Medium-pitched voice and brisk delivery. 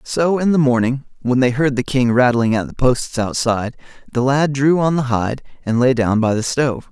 No: low, 130 Hz; fast, 225 wpm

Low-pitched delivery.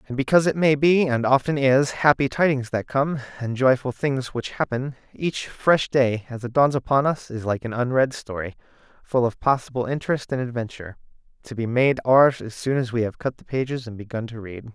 Yes: low, 130 Hz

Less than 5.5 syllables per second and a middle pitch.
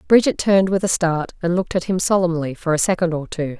No: 6.3 syllables/s; medium, 175 Hz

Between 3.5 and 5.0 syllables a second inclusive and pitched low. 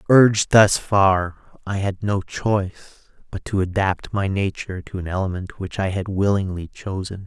Yes: 4.8 syllables/s; very low, 95 Hz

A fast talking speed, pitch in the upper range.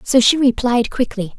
No: average, 175 wpm; high, 245 Hz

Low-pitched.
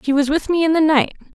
No: very high, 300 Hz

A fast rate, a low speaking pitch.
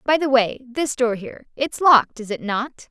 No: fast, 225 wpm; very high, 250 Hz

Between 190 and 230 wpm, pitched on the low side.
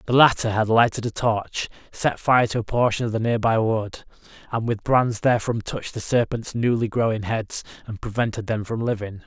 Yes: average, 195 wpm; low, 115 Hz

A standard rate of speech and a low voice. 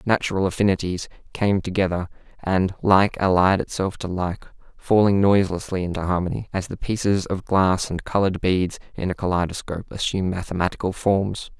Yes: average, 145 wpm; very low, 95 Hz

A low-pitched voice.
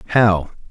Yes: low, 100 Hz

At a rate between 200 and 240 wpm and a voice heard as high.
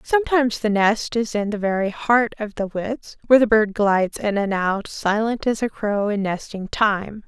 Yes: fast, 205 wpm; high, 215 Hz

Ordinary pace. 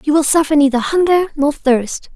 Yes: average, 195 wpm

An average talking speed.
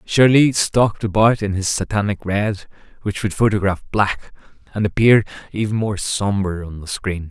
Yes: average, 155 wpm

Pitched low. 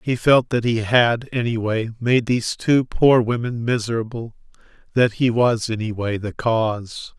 Yes: low, 115 Hz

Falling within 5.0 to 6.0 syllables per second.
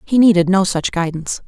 Yes: 5.9 syllables/s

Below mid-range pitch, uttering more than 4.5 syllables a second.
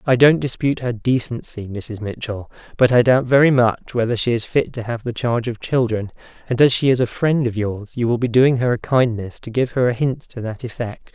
Yes: low, 120 Hz; 5.4 syllables/s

